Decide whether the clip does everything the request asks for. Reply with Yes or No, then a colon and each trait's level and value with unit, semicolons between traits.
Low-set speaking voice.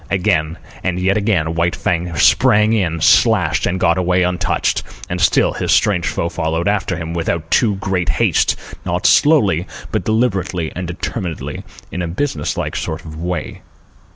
Yes: very low, 90 Hz